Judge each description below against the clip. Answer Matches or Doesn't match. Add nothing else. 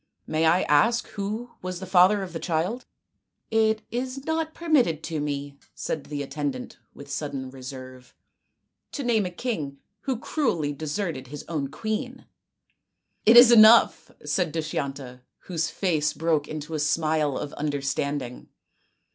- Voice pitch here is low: Doesn't match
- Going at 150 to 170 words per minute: Matches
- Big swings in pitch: Matches